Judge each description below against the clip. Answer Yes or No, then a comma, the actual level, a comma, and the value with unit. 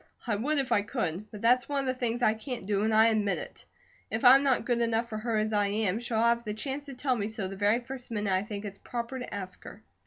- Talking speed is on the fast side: Yes, fast, 280 wpm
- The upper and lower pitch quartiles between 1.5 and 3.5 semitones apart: Yes, average, 3.0 semitones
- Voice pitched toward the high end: Yes, high, 225 Hz